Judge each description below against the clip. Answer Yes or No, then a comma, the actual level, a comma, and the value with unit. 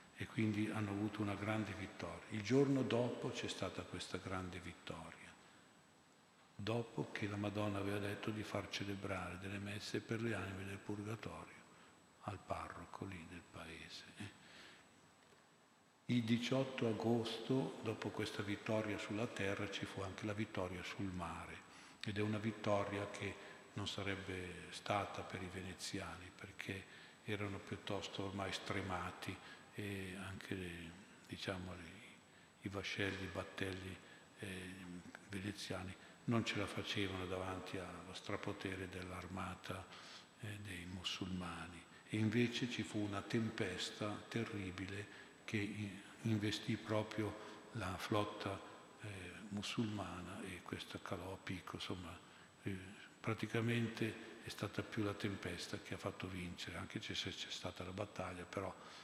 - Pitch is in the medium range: No, low, 100 Hz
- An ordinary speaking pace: Yes, average, 125 wpm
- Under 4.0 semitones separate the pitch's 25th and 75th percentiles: Yes, narrow, 2.5 semitones